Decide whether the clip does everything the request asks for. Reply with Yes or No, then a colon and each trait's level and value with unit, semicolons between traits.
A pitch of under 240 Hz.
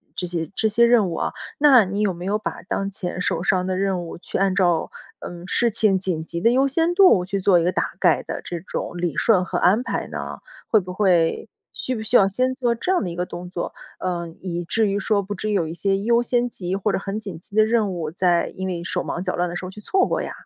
Yes: high, 190 Hz